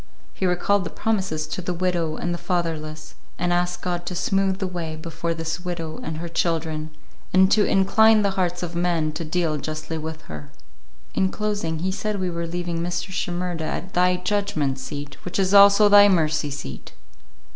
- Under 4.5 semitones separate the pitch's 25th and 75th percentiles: Yes, average, 2.9 semitones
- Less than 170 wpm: No, average, 185 wpm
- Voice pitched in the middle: Yes, medium, 175 Hz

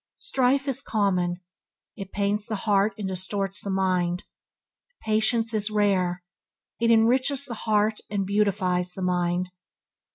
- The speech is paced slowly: Yes, slow, 130 wpm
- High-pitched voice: Yes, high, 205 Hz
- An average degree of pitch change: Yes, average, 3.1 semitones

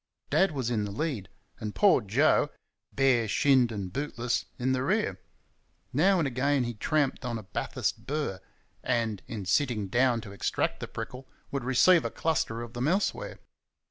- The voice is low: Yes, low, 125 Hz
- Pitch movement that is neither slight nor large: Yes, average, 4.2 semitones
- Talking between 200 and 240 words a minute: No, average, 170 wpm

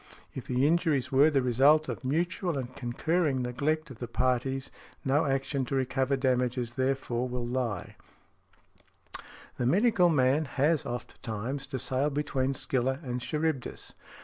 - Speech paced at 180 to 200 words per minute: No, average, 145 wpm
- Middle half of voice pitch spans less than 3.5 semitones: Yes, average, 2.8 semitones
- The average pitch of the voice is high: No, low, 135 Hz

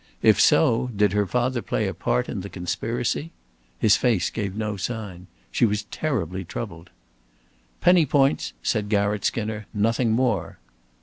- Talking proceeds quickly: No, average, 145 wpm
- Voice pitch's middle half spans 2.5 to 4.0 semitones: Yes, average, 3.5 semitones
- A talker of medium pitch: No, low, 105 Hz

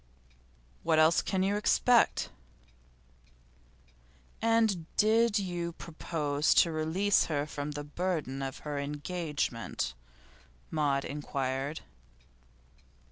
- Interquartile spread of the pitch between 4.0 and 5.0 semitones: Yes, average, 4.4 semitones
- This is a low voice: No, medium, 155 Hz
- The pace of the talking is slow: Yes, slow, 90 wpm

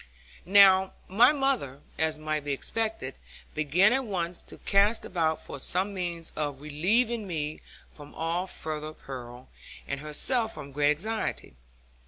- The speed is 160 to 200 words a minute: No, average, 140 wpm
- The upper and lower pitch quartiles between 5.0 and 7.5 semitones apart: Yes, wide, 5.4 semitones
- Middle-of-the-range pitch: Yes, medium, 165 Hz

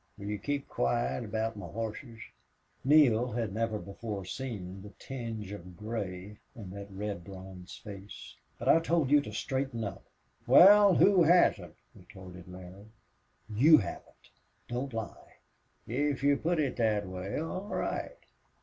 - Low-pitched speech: Yes, low, 110 Hz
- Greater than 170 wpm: No, average, 145 wpm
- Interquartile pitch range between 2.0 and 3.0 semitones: No, wide, 5.6 semitones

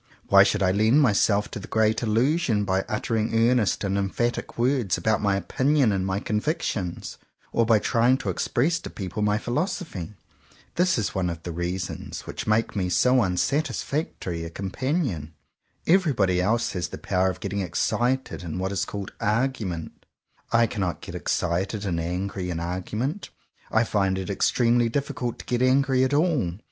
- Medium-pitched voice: No, low, 105 Hz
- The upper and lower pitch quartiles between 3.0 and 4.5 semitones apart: No, average, 5.0 semitones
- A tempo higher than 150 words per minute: Yes, average, 170 wpm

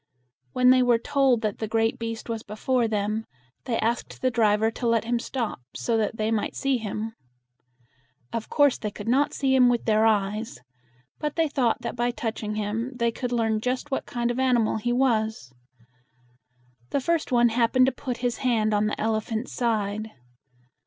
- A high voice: Yes, high, 230 Hz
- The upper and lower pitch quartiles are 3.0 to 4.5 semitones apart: No, narrow, 2.4 semitones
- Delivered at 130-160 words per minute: No, average, 185 wpm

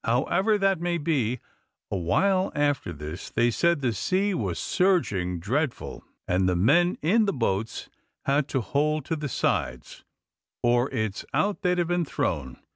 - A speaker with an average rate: Yes, average, 160 wpm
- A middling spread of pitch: No, wide, 8.5 semitones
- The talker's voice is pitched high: No, medium, 140 Hz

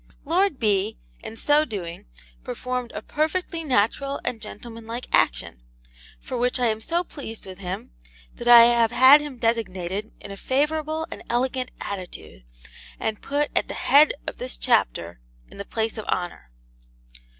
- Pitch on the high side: Yes, high, 235 Hz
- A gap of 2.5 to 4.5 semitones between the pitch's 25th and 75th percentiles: No, average, 5.3 semitones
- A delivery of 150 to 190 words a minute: Yes, average, 155 wpm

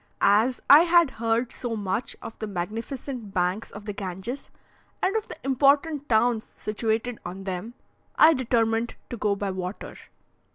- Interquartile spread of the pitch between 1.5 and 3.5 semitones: No, average, 4.1 semitones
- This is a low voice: No, high, 225 Hz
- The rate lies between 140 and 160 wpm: Yes, average, 155 wpm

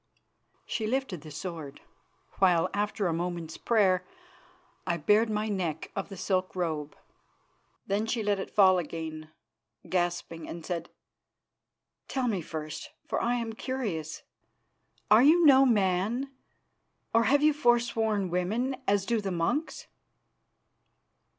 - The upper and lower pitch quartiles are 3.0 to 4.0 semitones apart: No, average, 5.2 semitones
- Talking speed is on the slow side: Yes, slow, 130 wpm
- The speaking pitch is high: Yes, high, 195 Hz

